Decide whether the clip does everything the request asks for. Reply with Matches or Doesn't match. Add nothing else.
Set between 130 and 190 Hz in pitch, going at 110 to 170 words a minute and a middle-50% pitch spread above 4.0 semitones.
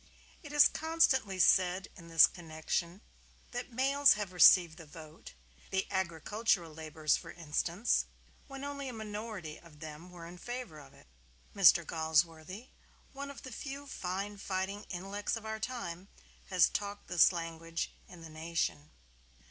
Matches